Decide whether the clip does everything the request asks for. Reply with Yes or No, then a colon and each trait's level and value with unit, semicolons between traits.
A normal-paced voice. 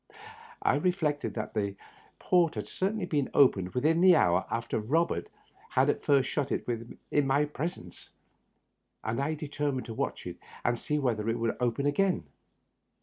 Yes: average, 160 wpm